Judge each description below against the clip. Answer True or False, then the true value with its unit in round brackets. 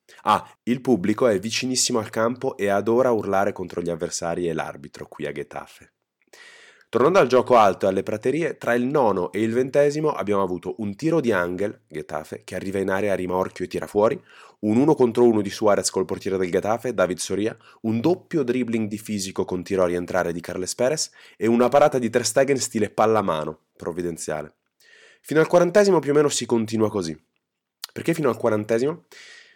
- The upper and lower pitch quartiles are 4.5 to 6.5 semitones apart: True (5.3 semitones)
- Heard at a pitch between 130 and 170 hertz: False (110 Hz)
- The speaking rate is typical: False (190 wpm)